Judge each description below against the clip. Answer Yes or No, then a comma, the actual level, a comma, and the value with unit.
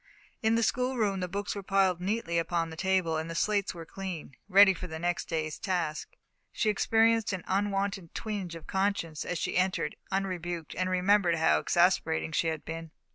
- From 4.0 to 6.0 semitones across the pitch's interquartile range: No, average, 3.3 semitones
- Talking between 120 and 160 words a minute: No, average, 185 wpm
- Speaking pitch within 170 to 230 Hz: Yes, medium, 185 Hz